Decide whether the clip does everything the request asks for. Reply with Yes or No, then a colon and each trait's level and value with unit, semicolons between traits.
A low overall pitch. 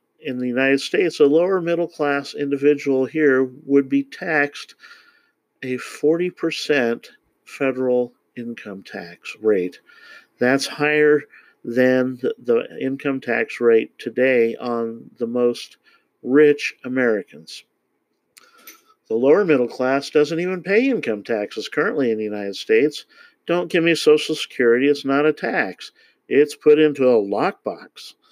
No: medium, 145 Hz